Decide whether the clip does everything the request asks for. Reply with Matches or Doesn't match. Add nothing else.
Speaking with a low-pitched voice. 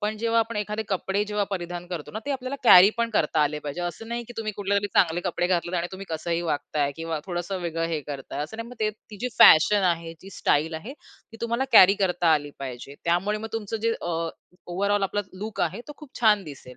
Doesn't match